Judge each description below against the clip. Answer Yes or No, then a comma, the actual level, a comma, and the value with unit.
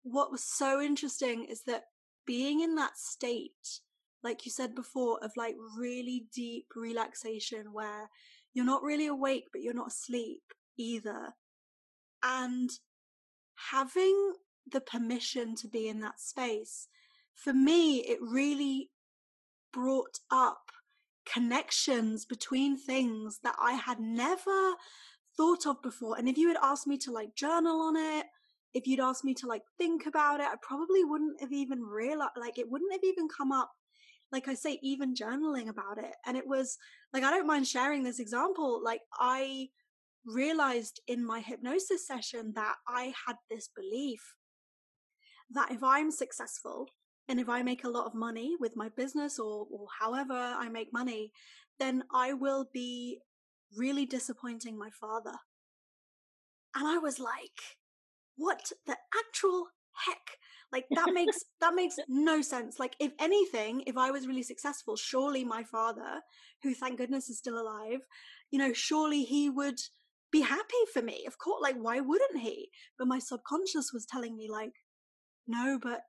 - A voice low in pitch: No, very high, 265 Hz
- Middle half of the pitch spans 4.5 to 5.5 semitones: No, average, 3.7 semitones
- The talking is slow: No, average, 160 wpm